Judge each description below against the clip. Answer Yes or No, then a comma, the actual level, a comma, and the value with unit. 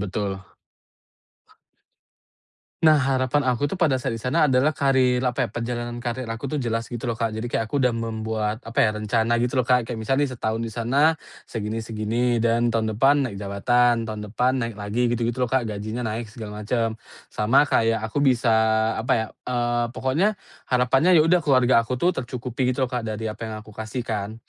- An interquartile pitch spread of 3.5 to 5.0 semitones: No, narrow, 2.5 semitones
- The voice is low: Yes, low, 120 Hz